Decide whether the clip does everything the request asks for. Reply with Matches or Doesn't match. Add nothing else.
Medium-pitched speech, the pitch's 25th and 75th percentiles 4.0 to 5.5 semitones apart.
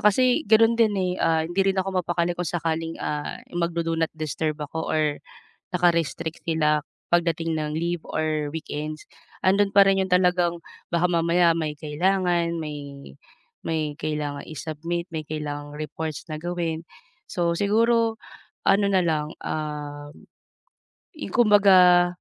Doesn't match